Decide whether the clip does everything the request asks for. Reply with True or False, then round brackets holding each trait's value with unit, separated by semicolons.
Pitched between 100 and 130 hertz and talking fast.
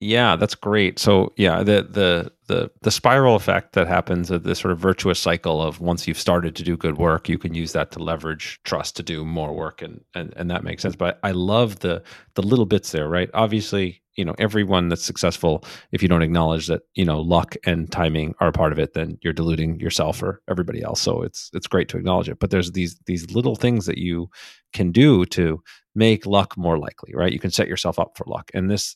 False (90 Hz; 235 wpm)